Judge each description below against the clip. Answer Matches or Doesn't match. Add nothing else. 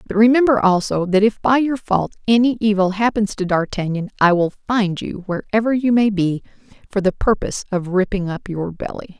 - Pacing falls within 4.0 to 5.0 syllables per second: Doesn't match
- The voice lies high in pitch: Matches